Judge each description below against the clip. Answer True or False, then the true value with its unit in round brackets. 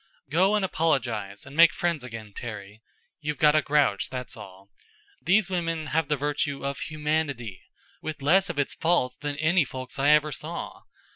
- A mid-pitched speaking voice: True (145 Hz)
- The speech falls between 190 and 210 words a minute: False (170 wpm)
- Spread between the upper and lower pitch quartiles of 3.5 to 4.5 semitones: True (4.1 semitones)